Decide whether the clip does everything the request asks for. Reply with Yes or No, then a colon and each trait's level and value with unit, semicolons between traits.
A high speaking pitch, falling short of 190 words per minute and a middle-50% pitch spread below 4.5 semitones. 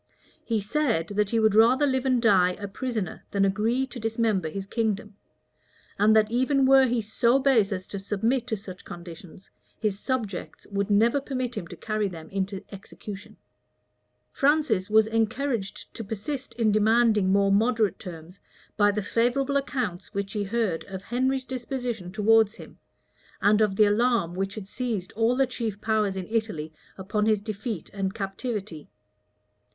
Yes: high, 215 Hz; average, 165 wpm; average, 3.5 semitones